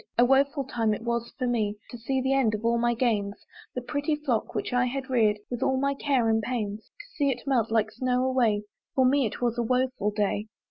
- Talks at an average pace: No, fast, 235 wpm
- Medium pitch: No, high, 245 Hz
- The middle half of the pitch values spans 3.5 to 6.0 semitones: No, average, 2.9 semitones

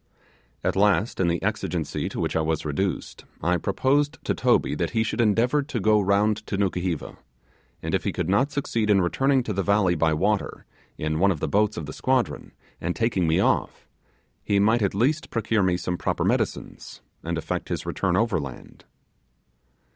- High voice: No, low, 100 Hz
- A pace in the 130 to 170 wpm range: No, average, 185 wpm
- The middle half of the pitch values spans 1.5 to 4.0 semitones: No, average, 4.4 semitones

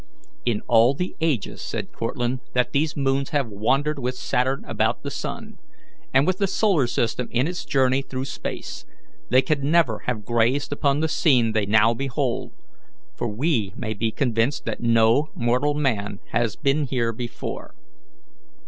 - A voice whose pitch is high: No, low, 125 Hz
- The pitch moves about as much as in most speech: Yes, average, 3.8 semitones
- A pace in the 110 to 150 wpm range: No, average, 160 wpm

